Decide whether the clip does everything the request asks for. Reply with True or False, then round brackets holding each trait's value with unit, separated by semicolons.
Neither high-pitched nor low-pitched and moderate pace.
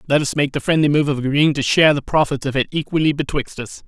False (145 Hz; 265 wpm)